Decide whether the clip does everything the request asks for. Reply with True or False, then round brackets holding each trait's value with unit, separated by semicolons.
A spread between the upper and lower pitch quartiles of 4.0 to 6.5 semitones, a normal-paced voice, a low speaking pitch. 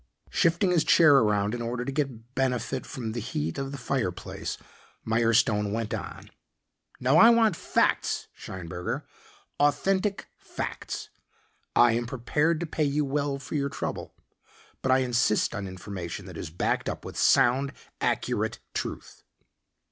True (4.7 semitones; 145 wpm; 125 Hz)